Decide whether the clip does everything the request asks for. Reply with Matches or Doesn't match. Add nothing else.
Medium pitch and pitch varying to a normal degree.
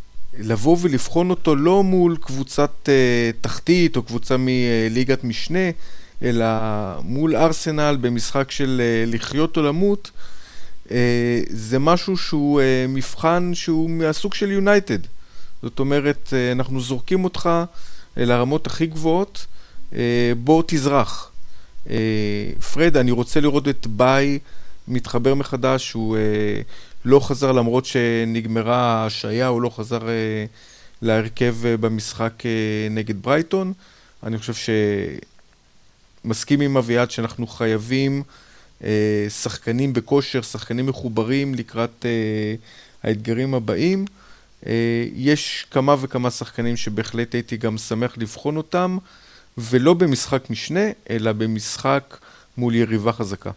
Doesn't match